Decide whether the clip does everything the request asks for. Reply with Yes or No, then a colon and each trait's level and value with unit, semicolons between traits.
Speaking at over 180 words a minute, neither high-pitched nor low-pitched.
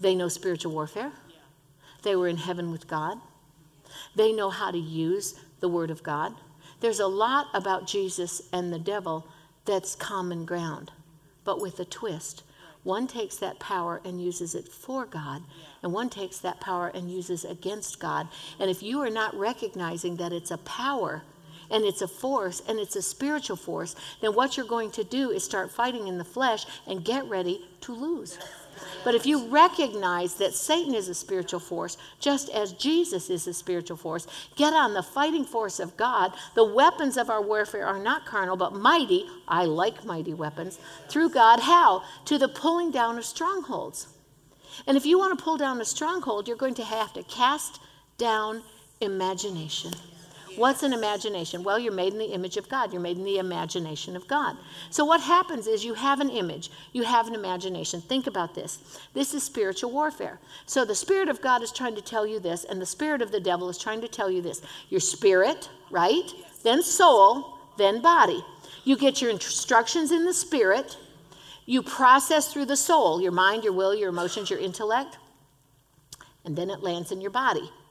No: average, 190 wpm; high, 200 Hz